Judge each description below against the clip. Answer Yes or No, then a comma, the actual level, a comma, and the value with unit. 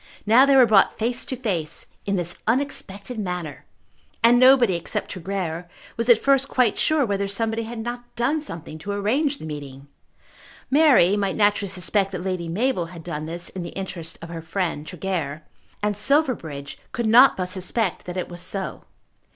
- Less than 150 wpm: No, average, 175 wpm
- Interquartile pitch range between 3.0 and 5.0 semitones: No, wide, 5.6 semitones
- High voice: Yes, high, 195 Hz